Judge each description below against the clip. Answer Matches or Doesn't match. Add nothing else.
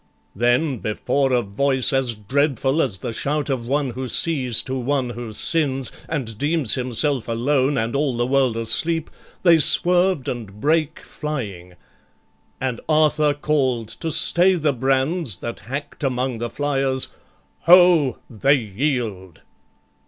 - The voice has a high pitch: Doesn't match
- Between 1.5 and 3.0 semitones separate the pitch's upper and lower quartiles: Doesn't match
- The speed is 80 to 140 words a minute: Matches